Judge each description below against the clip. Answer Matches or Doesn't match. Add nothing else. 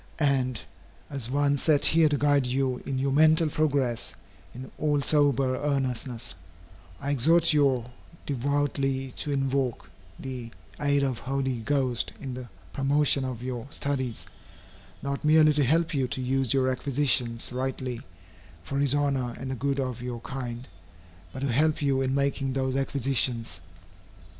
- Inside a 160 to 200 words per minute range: Doesn't match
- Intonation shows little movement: Matches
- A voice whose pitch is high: Doesn't match